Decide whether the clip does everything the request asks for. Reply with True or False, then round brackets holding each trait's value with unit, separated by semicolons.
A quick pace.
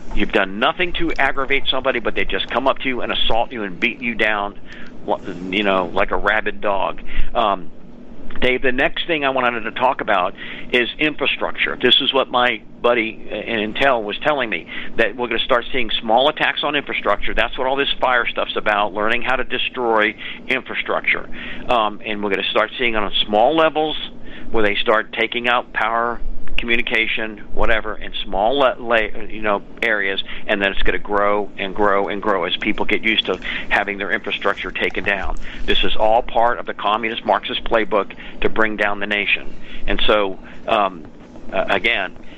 False (190 wpm)